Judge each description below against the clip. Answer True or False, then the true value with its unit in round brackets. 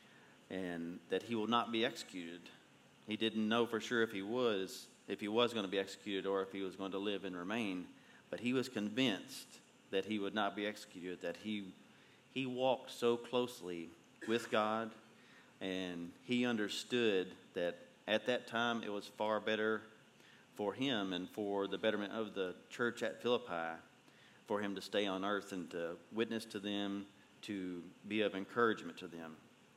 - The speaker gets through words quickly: False (175 wpm)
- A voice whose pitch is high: False (105 Hz)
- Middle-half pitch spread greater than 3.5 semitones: False (2.8 semitones)